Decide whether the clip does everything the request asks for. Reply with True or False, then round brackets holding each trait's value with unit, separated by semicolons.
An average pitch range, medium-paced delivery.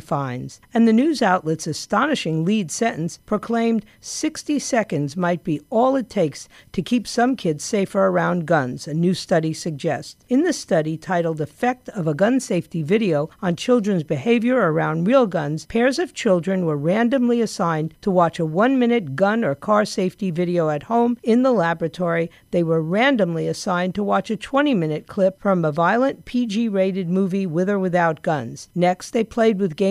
False (5.8 semitones; 180 wpm)